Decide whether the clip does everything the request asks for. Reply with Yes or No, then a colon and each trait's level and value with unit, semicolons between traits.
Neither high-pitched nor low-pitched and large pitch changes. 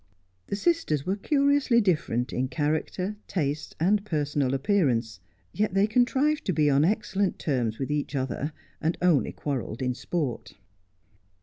Yes: medium, 155 Hz; wide, 7.0 semitones